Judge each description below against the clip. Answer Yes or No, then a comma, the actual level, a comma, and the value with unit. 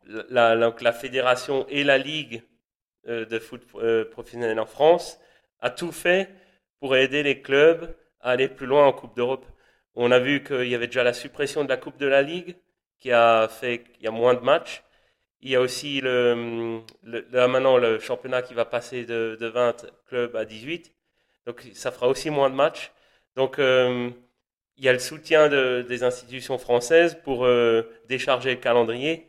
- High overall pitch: No, low, 125 Hz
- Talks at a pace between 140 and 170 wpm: No, average, 190 wpm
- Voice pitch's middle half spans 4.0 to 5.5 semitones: No, average, 2.9 semitones